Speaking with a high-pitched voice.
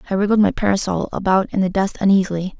Yes: high, 195 Hz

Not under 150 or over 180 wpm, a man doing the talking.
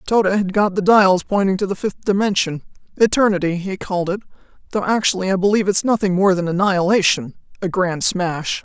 No: average, 175 wpm; female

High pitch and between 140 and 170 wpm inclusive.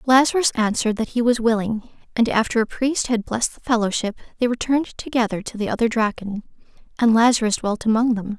No: high, 230 Hz; average, 185 wpm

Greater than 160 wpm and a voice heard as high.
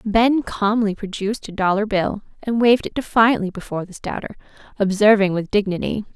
No: average, 155 wpm; high, 210 Hz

